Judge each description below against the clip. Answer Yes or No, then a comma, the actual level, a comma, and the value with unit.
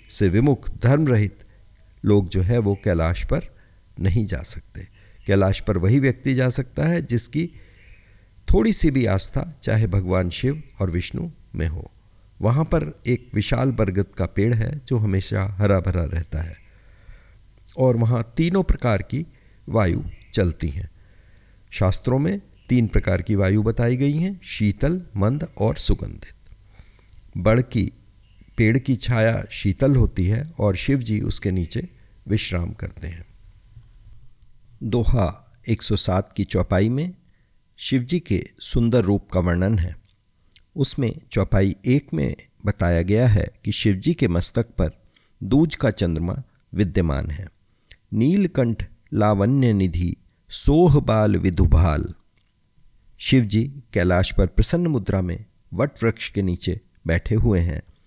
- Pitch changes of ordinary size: Yes, average, 4.3 semitones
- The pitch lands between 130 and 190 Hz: No, low, 105 Hz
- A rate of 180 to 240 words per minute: No, average, 135 wpm